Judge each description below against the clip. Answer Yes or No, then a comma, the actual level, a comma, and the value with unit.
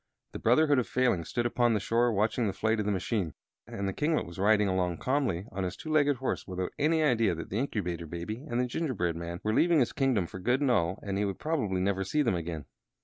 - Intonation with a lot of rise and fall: Yes, wide, 5.7 semitones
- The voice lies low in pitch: Yes, low, 105 Hz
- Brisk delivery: Yes, fast, 245 wpm